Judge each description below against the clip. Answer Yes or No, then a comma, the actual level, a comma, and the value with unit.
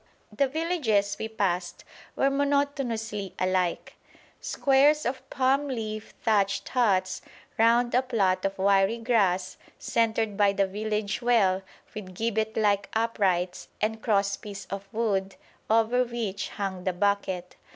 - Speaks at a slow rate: Yes, slow, 130 wpm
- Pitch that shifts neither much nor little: Yes, average, 3.3 semitones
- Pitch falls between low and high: No, high, 215 Hz